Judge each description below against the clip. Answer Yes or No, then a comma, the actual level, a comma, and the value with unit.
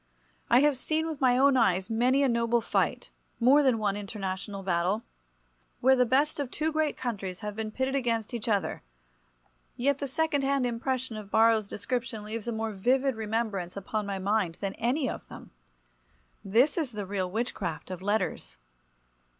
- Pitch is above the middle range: Yes, high, 225 Hz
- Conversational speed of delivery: Yes, average, 170 wpm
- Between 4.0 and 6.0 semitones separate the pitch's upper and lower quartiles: Yes, average, 4.7 semitones